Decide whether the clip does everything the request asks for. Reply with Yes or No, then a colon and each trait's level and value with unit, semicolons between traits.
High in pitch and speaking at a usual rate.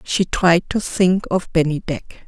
No: medium, 175 Hz; average, 160 wpm